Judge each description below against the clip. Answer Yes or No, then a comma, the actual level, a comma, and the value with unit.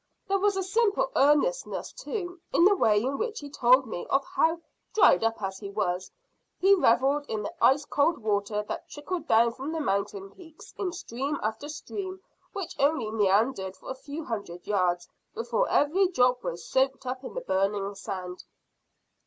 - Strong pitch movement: Yes, wide, 8.5 semitones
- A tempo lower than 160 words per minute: No, average, 175 wpm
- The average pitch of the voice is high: Yes, very high, 265 Hz